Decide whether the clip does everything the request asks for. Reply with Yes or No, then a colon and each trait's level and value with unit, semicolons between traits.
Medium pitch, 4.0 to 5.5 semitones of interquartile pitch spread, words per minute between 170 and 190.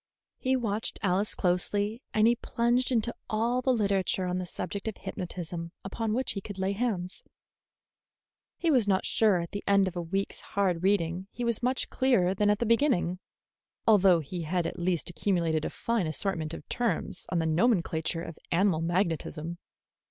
No: high, 195 Hz; average, 4.3 semitones; average, 180 wpm